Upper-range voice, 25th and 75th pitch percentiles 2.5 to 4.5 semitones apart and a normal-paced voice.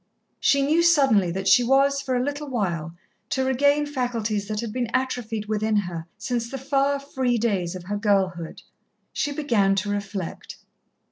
No: high, 235 Hz; average, 5.2 semitones; average, 165 wpm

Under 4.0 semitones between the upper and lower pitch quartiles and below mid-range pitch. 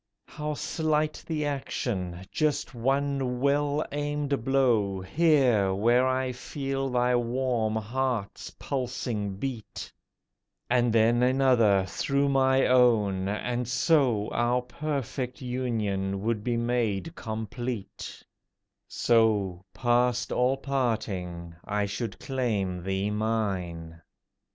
No: average, 4.3 semitones; low, 120 Hz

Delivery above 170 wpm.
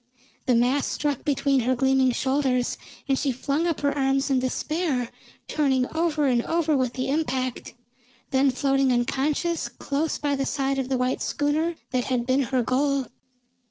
No: average, 165 wpm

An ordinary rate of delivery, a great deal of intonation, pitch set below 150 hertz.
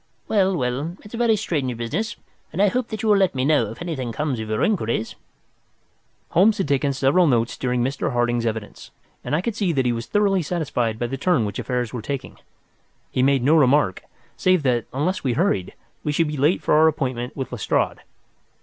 No: fast, 215 wpm; wide, 6.6 semitones; medium, 140 Hz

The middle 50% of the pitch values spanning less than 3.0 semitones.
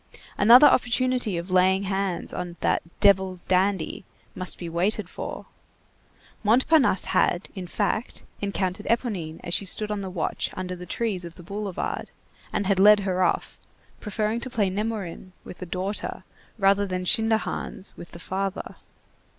Yes: narrow, 2.6 semitones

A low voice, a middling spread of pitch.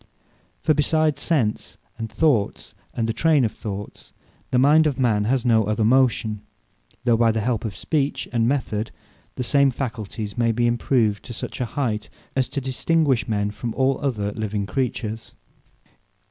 Yes: low, 120 Hz; average, 3.8 semitones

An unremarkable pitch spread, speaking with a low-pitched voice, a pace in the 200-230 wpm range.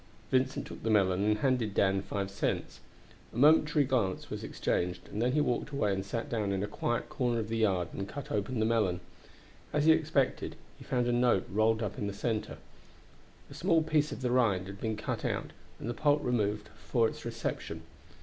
Yes: average, 4.3 semitones; low, 115 Hz; fast, 205 wpm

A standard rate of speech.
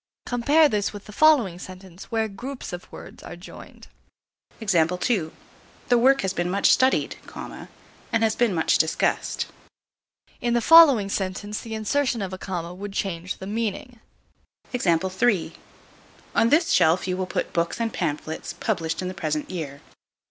Yes: average, 150 wpm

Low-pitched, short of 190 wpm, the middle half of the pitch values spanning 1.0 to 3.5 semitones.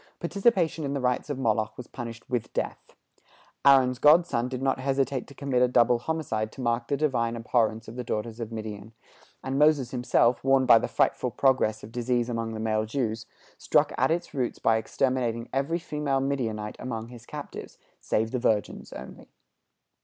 Yes: low, 125 Hz; average, 180 wpm; average, 3.2 semitones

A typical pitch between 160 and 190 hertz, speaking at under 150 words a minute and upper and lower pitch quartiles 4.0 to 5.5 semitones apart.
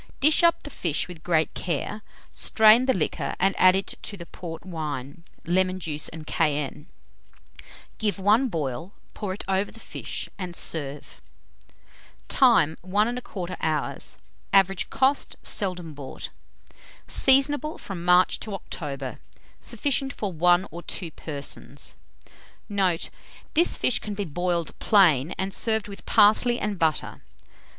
Yes: medium, 185 Hz; slow, 135 wpm; average, 4.7 semitones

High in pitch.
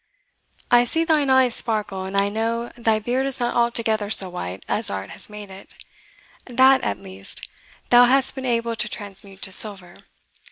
Yes: high, 225 Hz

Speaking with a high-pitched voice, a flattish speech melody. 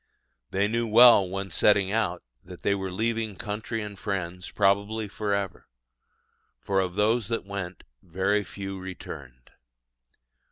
No: low, 100 Hz; narrow, 2.2 semitones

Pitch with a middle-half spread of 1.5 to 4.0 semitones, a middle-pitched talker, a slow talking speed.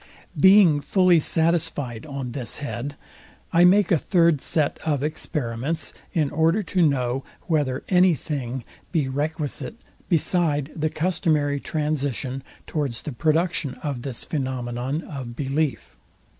Yes: average, 3.6 semitones; medium, 150 Hz; slow, 125 wpm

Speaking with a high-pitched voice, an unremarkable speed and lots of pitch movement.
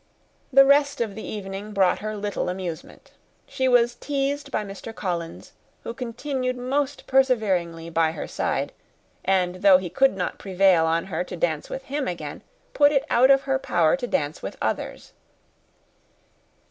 Yes: high, 210 Hz; average, 160 wpm; wide, 6.8 semitones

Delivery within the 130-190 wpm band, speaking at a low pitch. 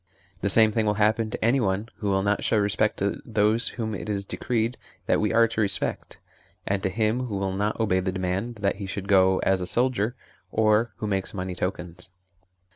No: fast, 205 wpm; low, 105 Hz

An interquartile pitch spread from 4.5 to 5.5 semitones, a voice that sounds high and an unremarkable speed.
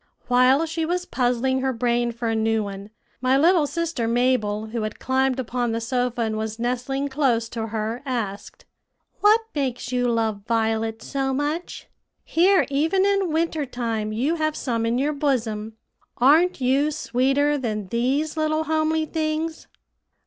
Yes: average, 5.0 semitones; very high, 255 Hz; average, 155 wpm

